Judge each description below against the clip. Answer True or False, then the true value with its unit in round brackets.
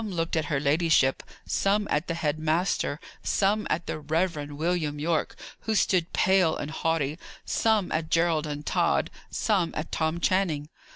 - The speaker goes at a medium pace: True (165 wpm)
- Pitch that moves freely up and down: False (3.1 semitones)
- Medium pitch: True (165 Hz)